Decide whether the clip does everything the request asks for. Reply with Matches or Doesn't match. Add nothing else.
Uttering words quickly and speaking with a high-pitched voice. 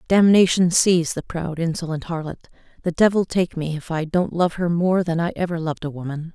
Doesn't match